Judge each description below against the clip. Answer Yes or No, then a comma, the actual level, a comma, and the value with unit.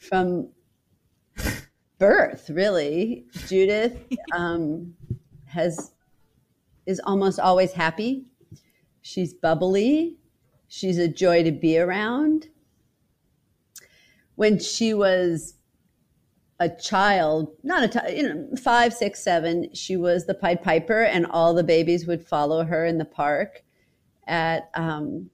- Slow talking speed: Yes, slow, 110 wpm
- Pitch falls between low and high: Yes, medium, 175 Hz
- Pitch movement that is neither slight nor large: Yes, average, 4.3 semitones